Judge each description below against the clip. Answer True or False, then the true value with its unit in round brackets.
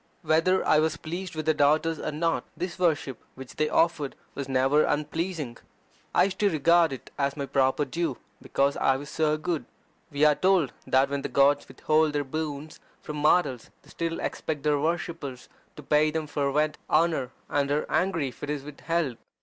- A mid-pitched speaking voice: True (150 Hz)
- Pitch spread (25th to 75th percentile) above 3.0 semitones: False (2.7 semitones)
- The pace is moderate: True (185 wpm)